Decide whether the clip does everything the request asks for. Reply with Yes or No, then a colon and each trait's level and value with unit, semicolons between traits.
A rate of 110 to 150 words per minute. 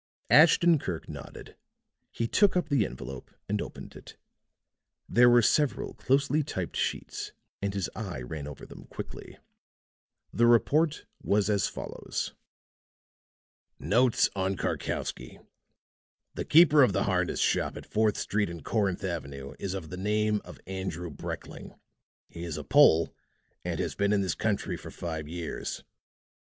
Yes: average, 145 wpm